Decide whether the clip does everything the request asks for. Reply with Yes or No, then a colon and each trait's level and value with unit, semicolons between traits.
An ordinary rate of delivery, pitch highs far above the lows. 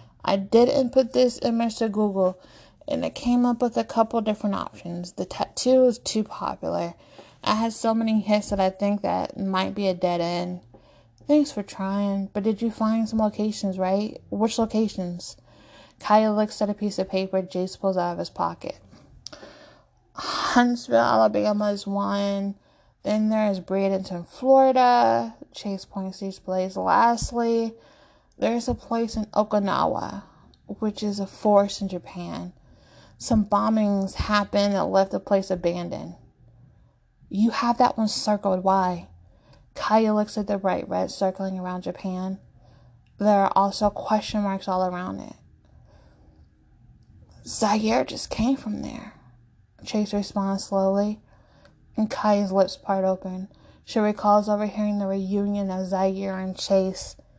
No: average, 145 wpm; narrow, 2.6 semitones